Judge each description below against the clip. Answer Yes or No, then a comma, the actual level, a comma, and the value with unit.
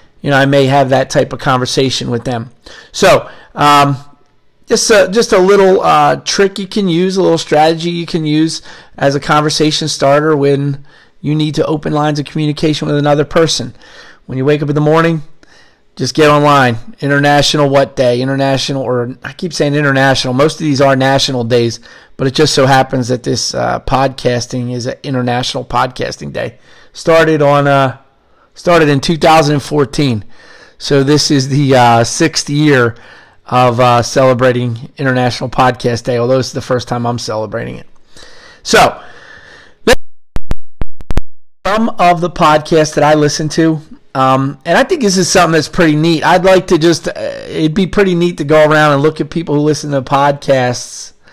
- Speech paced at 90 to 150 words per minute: No, average, 175 wpm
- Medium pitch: Yes, medium, 145 Hz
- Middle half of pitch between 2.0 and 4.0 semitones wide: Yes, average, 3.3 semitones